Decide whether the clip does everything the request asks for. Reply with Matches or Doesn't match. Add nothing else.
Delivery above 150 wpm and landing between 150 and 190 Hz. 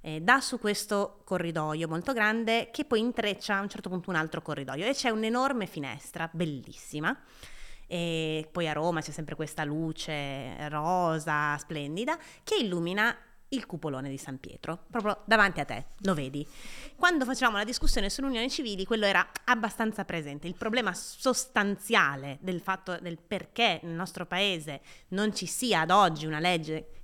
Matches